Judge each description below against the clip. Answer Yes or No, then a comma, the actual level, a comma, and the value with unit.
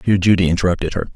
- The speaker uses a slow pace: No, fast, 205 wpm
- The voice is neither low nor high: No, very low, 90 Hz